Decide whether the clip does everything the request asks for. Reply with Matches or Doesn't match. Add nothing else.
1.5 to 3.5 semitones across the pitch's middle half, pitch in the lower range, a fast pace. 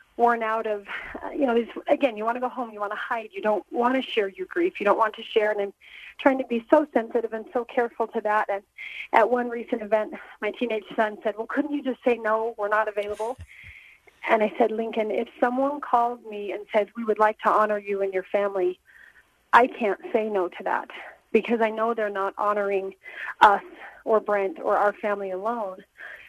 Doesn't match